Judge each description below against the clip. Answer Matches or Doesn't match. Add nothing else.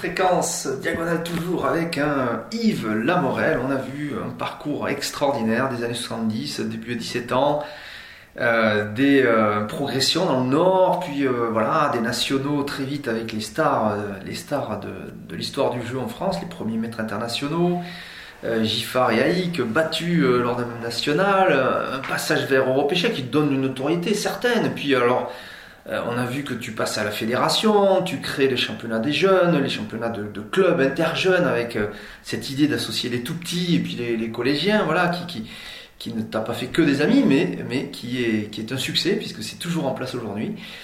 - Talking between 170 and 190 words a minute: Matches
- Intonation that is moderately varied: Doesn't match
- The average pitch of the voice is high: Doesn't match